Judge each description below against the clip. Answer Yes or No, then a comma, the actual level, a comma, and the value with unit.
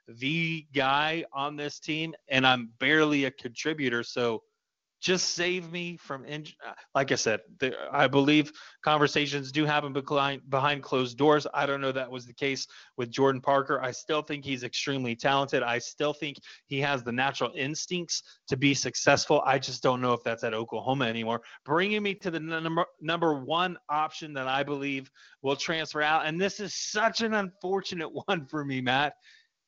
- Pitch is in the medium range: Yes, medium, 145 Hz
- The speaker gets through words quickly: No, average, 180 wpm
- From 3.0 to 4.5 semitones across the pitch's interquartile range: Yes, average, 3.4 semitones